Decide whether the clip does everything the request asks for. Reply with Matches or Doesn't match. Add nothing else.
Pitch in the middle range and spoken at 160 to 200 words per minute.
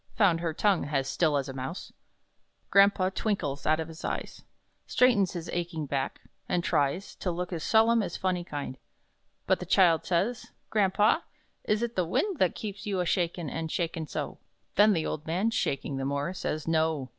Matches